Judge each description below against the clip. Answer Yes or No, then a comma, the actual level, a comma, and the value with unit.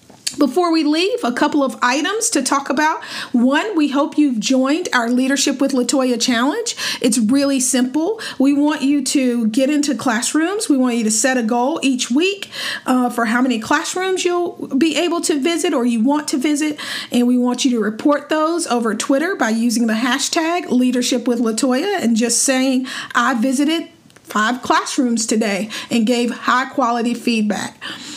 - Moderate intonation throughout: Yes, average, 3.9 semitones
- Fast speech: No, average, 175 wpm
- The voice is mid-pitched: No, very high, 270 Hz